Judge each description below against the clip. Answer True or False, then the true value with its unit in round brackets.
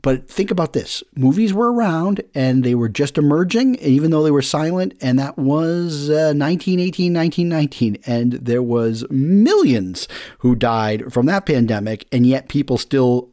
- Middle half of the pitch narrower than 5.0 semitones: False (5.3 semitones)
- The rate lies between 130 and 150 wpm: False (160 wpm)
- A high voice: False (140 Hz)